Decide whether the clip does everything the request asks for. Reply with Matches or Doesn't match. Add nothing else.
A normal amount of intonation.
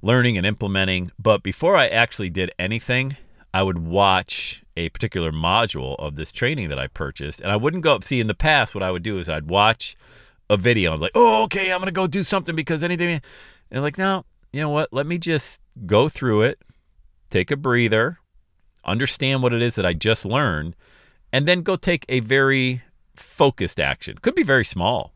Doesn't match